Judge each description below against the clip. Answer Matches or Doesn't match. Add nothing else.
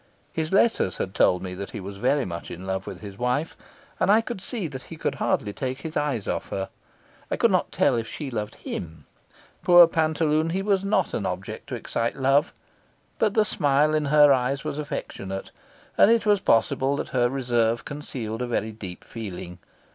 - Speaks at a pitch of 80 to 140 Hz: Matches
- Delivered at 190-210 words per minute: Matches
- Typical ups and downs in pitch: Doesn't match